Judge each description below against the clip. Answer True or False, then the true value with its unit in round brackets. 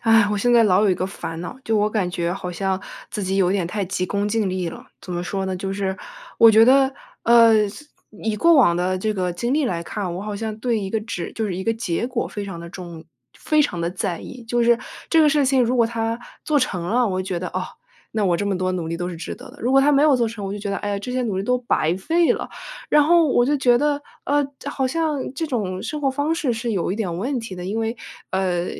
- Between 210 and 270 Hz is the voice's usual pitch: True (215 Hz)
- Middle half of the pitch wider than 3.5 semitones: True (5.1 semitones)